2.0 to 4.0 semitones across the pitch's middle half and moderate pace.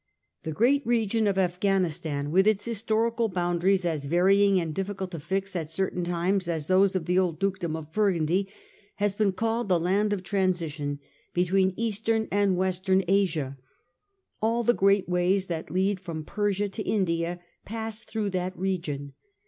Yes: average, 2.8 semitones; average, 160 wpm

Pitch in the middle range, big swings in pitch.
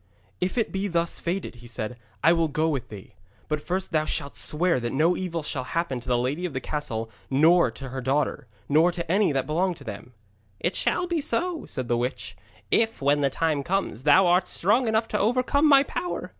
Yes: medium, 160 Hz; wide, 6.1 semitones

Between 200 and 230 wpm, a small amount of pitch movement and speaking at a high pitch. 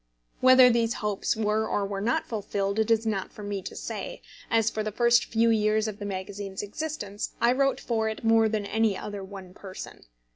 Yes: fast, 205 wpm; narrow, 2.0 semitones; high, 215 Hz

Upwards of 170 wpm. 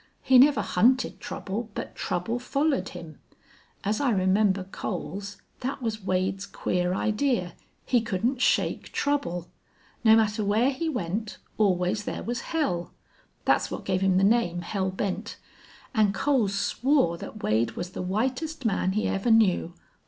No: average, 150 wpm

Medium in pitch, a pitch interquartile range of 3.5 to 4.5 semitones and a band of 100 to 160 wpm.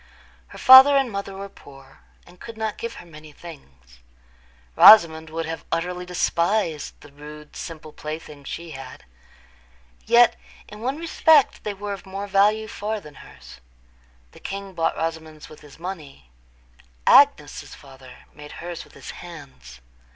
No: medium, 170 Hz; average, 5.2 semitones; average, 150 wpm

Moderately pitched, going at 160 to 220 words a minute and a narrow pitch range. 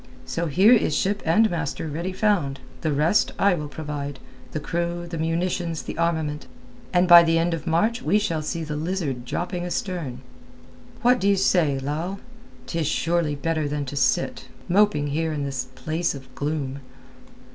No: medium, 165 Hz; average, 170 wpm; average, 3.2 semitones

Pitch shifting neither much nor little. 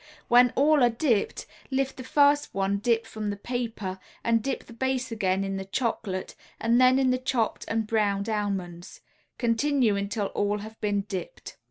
Yes: average, 4.1 semitones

